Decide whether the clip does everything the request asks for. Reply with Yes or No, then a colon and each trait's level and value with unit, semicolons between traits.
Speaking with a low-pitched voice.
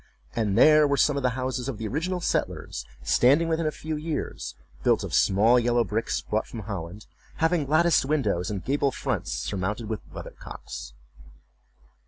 Yes: low, 125 Hz